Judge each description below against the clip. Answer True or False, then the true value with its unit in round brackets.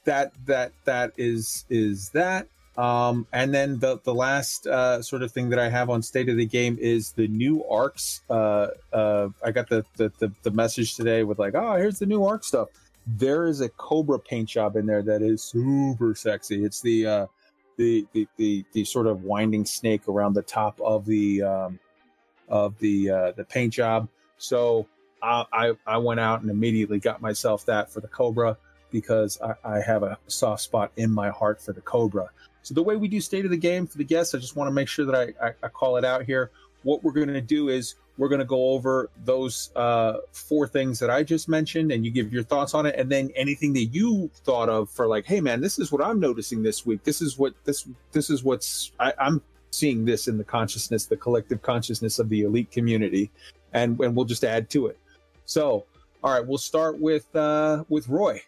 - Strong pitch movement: False (4.1 semitones)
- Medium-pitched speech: False (120 Hz)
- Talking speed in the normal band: False (220 wpm)